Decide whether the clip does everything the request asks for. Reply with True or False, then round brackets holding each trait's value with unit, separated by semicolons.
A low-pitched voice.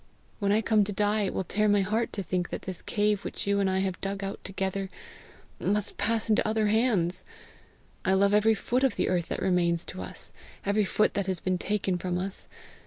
False (200 Hz)